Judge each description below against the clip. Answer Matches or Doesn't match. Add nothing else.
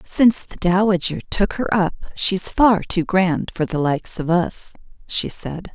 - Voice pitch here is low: Doesn't match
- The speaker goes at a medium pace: Matches